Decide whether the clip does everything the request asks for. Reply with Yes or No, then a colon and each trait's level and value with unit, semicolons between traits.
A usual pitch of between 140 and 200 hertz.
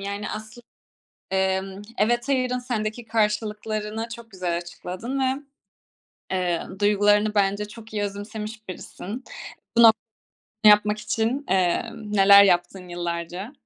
No: high, 210 Hz